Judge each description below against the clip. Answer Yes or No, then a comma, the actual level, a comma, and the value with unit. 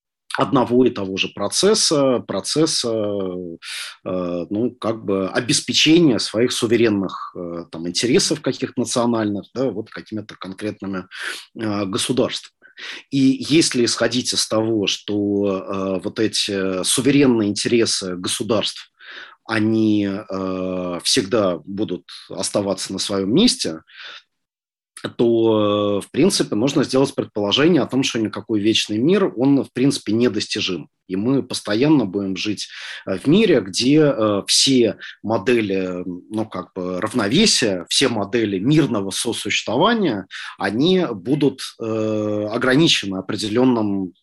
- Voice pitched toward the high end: No, low, 110 Hz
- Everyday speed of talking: No, slow, 105 wpm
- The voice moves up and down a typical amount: Yes, average, 4.4 semitones